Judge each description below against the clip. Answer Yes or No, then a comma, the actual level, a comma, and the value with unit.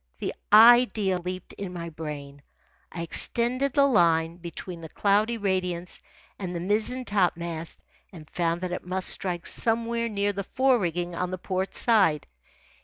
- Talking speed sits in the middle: Yes, average, 155 wpm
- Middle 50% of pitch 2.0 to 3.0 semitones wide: No, average, 4.0 semitones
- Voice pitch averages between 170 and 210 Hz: Yes, medium, 185 Hz